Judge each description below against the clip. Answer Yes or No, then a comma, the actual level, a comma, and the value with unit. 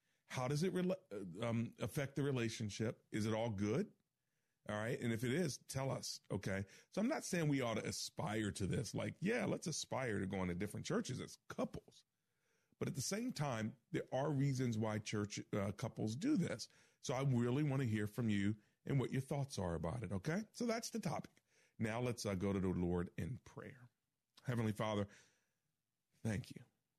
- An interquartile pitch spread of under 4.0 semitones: No, average, 5.1 semitones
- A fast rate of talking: No, average, 195 wpm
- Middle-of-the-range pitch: No, low, 120 Hz